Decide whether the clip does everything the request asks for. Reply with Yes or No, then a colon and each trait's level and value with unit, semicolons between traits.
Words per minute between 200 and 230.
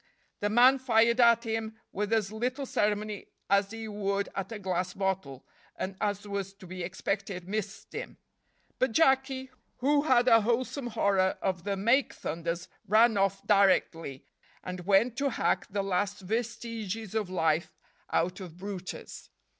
No: average, 155 wpm